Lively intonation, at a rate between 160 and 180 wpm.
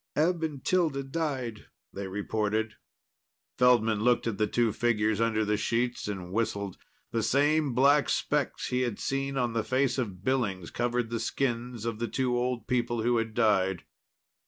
No: average, 3.3 semitones; average, 165 wpm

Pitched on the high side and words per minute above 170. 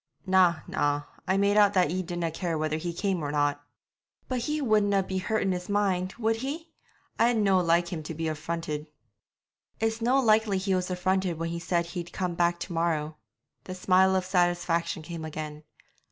No: medium, 180 Hz; average, 190 wpm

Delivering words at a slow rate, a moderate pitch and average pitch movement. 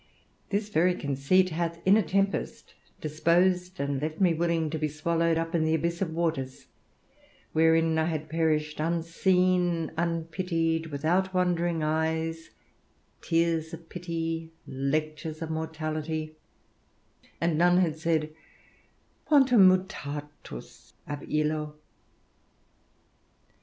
No: slow, 110 wpm; medium, 165 Hz; narrow, 1.9 semitones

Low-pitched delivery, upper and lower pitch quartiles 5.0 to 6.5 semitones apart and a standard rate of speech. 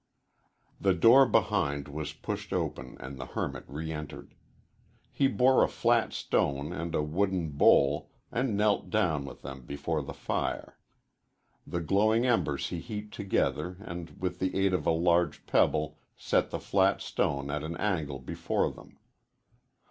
Yes: very low, 85 Hz; wide, 5.4 semitones; average, 155 wpm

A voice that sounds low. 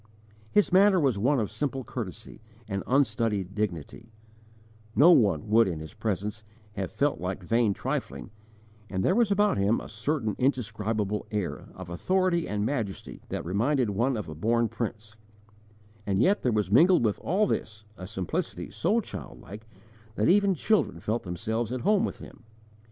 Yes: low, 110 Hz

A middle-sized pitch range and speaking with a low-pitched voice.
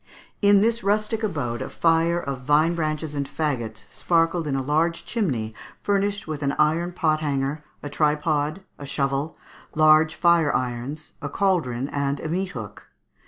No: average, 3.5 semitones; medium, 155 Hz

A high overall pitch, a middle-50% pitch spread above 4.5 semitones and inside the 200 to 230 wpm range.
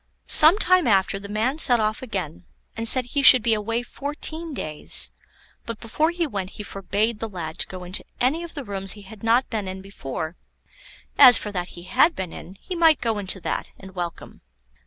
Yes: high, 220 Hz; wide, 5.6 semitones; fast, 205 wpm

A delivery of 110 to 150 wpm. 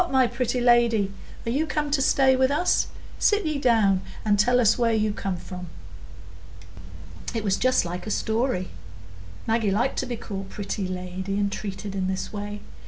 No: average, 175 wpm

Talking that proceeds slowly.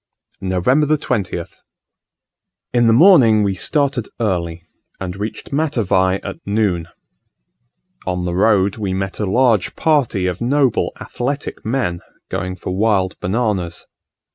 Yes: slow, 120 wpm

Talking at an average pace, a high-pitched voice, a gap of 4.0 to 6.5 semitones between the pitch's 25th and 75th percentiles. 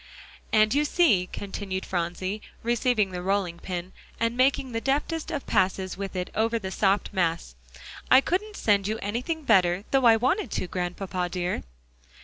Yes: average, 160 wpm; high, 205 Hz; average, 5.0 semitones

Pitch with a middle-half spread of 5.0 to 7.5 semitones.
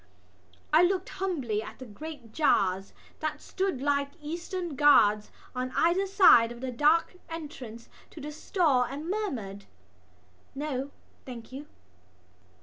Yes: wide, 5.6 semitones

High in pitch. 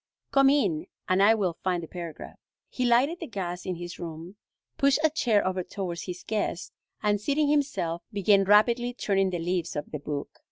Yes: high, 195 Hz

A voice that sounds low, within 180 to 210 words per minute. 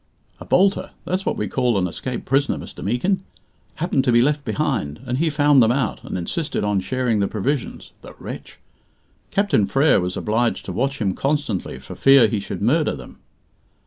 Yes: low, 125 Hz; average, 185 wpm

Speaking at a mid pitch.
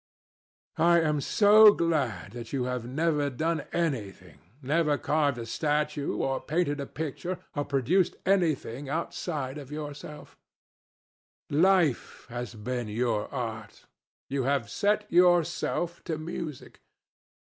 Yes: medium, 145 Hz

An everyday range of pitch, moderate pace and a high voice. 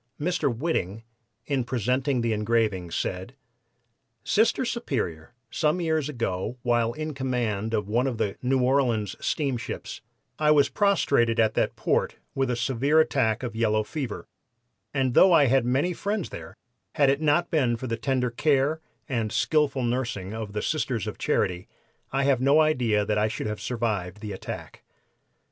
No: average, 4.4 semitones; average, 160 wpm; low, 125 Hz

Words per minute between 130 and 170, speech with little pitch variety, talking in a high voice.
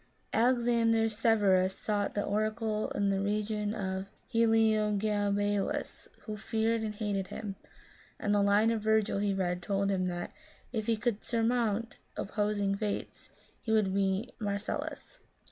Yes: average, 140 wpm; narrow, 1.9 semitones; high, 210 Hz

